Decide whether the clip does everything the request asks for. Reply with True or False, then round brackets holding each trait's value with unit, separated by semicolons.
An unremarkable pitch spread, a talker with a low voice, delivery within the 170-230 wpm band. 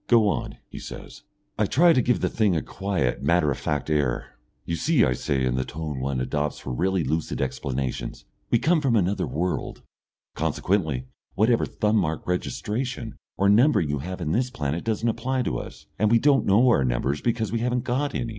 False (8.1 semitones; 95 Hz; 200 wpm)